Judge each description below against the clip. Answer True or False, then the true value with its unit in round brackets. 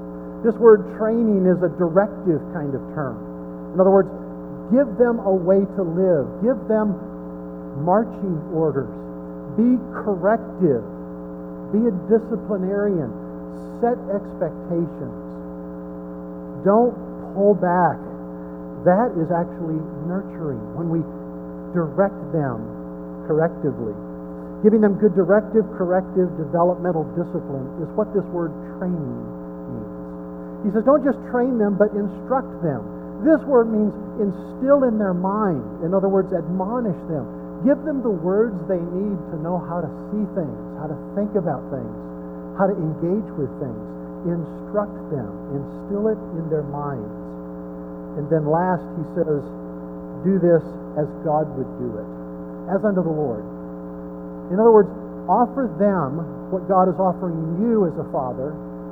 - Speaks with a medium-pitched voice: True (165 Hz)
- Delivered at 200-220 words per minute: False (135 wpm)